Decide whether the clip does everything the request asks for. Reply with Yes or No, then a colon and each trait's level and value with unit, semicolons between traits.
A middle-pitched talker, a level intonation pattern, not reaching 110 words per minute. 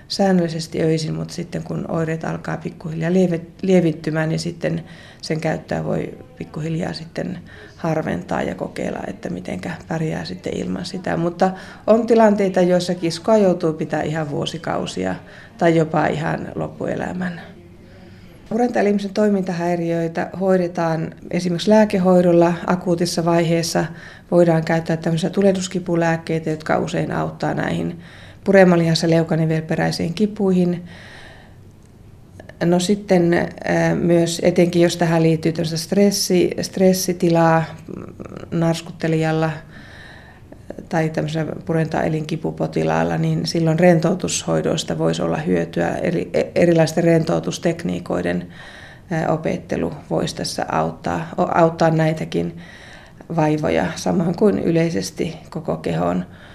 Yes: medium, 165 Hz; narrow, 2.2 semitones; average, 100 wpm